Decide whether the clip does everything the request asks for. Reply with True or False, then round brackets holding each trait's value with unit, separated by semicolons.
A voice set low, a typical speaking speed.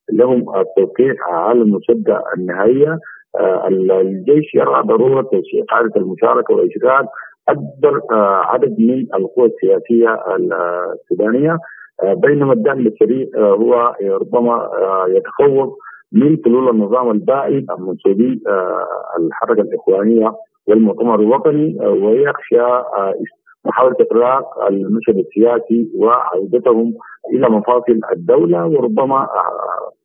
False (150 Hz; 85 wpm)